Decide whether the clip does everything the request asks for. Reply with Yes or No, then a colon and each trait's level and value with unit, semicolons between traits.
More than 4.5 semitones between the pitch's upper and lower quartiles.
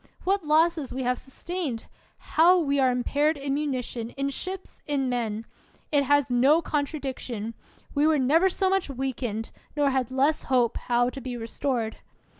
No: average, 3.6 semitones